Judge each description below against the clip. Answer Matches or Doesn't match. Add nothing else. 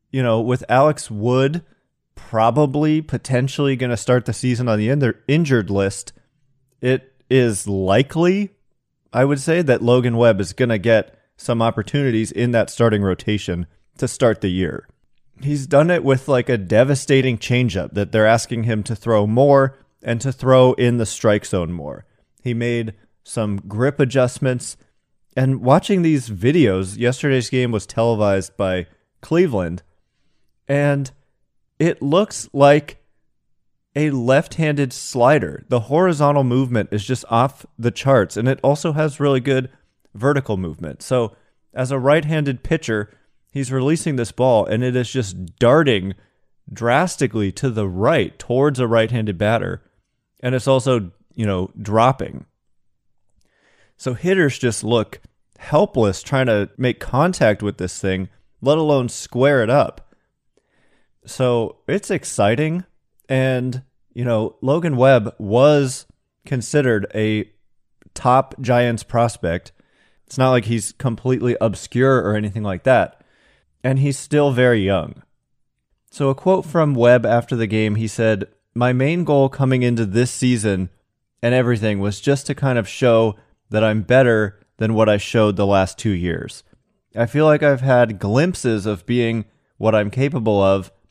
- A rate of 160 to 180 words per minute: Doesn't match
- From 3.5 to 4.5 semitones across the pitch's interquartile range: Matches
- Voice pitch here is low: Matches